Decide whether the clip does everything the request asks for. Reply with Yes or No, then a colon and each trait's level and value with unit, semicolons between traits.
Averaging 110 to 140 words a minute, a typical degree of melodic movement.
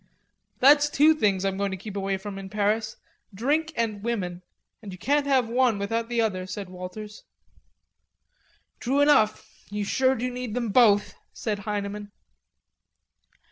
No: average, 150 wpm; average, 3.8 semitones